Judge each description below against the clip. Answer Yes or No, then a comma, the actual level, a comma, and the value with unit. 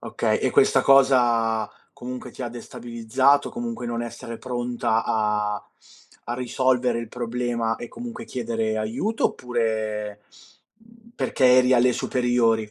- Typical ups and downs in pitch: No, narrow, 2.2 semitones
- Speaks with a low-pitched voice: Yes, low, 120 Hz